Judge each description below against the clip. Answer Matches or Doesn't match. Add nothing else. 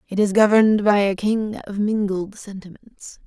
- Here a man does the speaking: Doesn't match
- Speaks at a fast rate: Doesn't match